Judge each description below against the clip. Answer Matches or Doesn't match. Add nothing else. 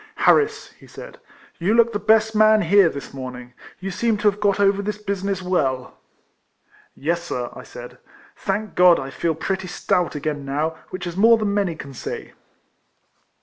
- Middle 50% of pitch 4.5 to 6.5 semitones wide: Matches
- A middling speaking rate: Matches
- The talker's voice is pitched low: Doesn't match